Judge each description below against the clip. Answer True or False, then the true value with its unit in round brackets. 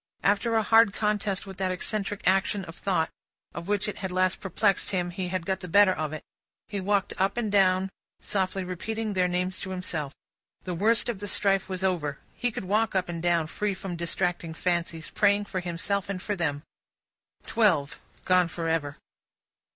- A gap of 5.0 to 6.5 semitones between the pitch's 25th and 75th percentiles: False (2.6 semitones)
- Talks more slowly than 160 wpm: False (180 wpm)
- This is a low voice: False (190 Hz)